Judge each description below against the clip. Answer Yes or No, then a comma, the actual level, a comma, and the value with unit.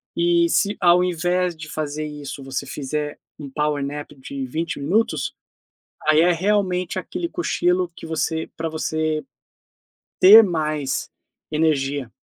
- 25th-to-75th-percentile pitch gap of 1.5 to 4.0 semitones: Yes, average, 3.2 semitones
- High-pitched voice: No, medium, 160 Hz